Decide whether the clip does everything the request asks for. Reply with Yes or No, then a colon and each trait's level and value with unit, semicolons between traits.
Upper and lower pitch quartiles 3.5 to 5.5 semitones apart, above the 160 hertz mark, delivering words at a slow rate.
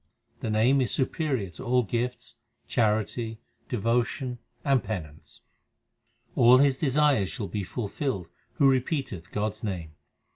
No: average, 4.1 semitones; low, 120 Hz; slow, 125 wpm